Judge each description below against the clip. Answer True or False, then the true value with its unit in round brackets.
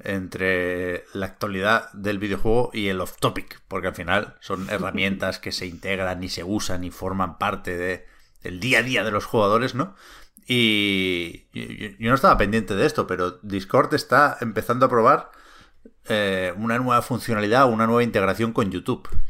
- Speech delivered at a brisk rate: False (170 wpm)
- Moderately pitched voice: False (100 Hz)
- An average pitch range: True (3.6 semitones)